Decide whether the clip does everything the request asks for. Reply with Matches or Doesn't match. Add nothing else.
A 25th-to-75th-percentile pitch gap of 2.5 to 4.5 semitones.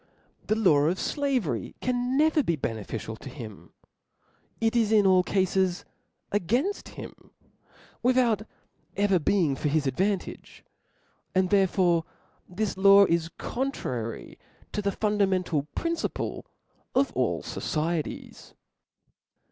Doesn't match